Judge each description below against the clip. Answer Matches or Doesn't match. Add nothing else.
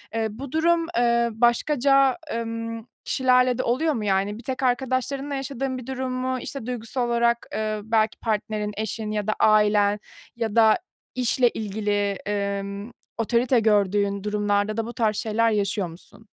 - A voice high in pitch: Matches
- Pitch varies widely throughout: Doesn't match